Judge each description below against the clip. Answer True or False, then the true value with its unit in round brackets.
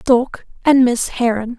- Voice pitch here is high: True (245 Hz)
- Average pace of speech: True (150 wpm)